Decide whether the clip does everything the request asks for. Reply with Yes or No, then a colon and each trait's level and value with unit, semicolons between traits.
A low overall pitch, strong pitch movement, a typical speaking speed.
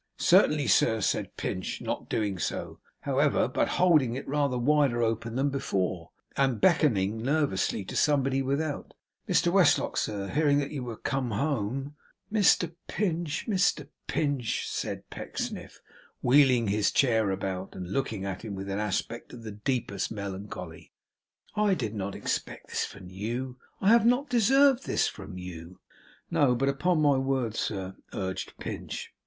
Yes: low, 125 Hz; wide, 6.4 semitones; average, 155 wpm